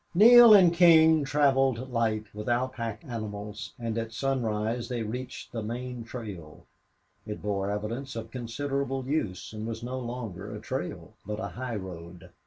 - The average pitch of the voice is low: Yes, low, 115 Hz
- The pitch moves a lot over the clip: No, average, 3.7 semitones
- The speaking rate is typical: Yes, average, 155 wpm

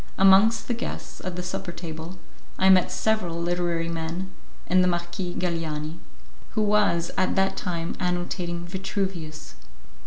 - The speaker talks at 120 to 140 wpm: Yes, slow, 135 wpm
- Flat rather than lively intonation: Yes, narrow, 2.1 semitones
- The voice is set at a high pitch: No, medium, 175 Hz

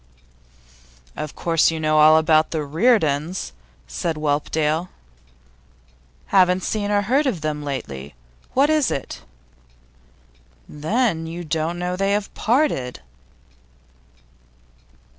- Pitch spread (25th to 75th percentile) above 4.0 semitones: Yes, average, 4.9 semitones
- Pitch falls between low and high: Yes, medium, 160 Hz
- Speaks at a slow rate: Yes, slow, 110 wpm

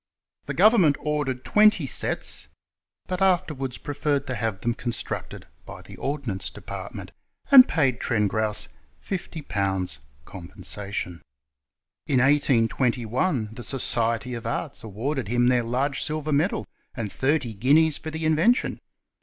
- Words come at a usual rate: No, slow, 125 wpm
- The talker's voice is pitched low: Yes, low, 130 Hz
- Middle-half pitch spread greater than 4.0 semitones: Yes, average, 5.2 semitones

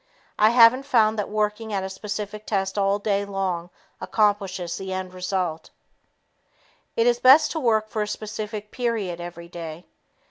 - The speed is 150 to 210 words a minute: Yes, average, 155 wpm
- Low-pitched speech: No, high, 205 Hz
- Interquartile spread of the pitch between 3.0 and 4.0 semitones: No, narrow, 2.6 semitones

